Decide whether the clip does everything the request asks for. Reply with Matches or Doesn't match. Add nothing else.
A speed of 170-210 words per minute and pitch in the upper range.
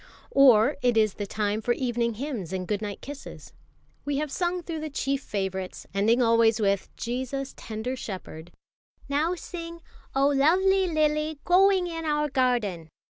Doesn't match